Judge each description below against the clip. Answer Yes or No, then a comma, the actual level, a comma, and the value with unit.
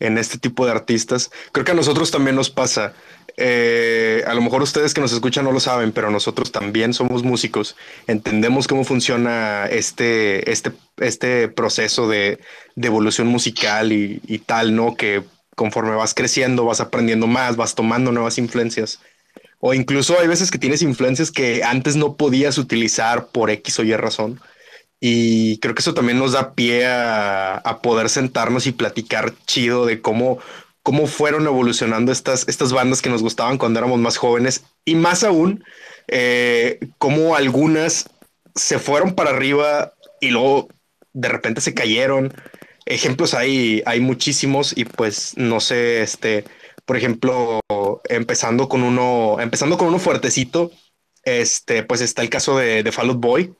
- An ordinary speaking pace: Yes, average, 160 wpm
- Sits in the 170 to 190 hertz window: No, low, 125 Hz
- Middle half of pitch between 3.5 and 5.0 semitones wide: No, average, 2.9 semitones